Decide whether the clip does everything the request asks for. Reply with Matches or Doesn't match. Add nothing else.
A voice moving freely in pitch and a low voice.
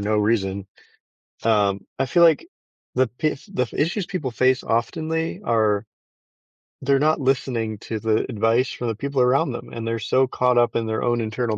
Doesn't match